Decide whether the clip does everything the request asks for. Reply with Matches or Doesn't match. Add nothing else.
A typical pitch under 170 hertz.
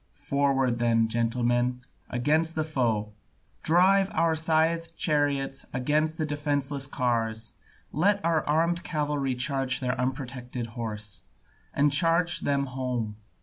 Matches